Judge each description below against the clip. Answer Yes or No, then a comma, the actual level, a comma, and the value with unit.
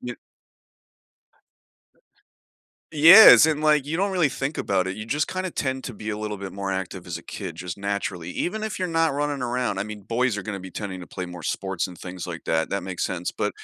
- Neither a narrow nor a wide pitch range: No, wide, 7.8 semitones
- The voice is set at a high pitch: No, low, 105 Hz